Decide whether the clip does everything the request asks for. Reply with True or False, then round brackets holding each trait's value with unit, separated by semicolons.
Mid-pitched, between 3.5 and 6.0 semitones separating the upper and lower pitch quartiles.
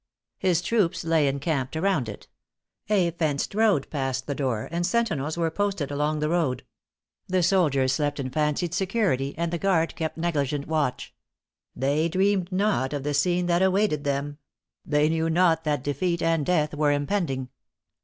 True (160 Hz; 3.8 semitones)